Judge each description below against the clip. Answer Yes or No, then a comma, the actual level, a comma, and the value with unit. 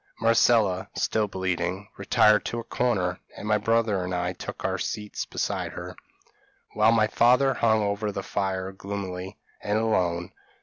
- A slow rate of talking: No, average, 150 wpm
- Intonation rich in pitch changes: No, average, 3.0 semitones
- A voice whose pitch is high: No, low, 100 Hz